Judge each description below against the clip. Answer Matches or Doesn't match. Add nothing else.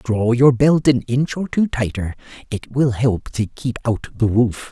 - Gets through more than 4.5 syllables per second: Doesn't match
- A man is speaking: Matches